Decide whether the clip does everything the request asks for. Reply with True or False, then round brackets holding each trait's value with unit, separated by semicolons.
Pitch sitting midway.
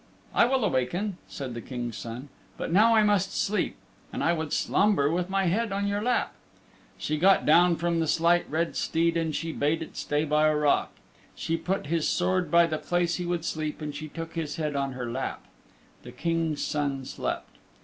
True (165 Hz)